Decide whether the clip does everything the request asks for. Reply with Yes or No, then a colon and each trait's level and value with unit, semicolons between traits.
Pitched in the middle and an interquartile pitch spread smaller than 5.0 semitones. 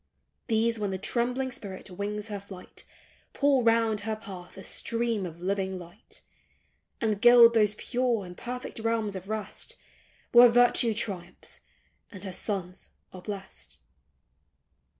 No: high, 210 Hz; average, 3.5 semitones